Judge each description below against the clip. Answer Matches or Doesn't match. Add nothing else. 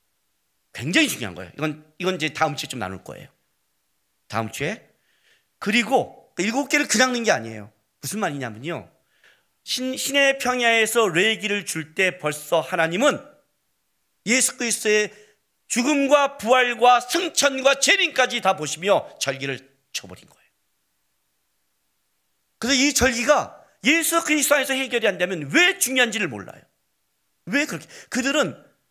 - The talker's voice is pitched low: Doesn't match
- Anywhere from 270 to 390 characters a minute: Matches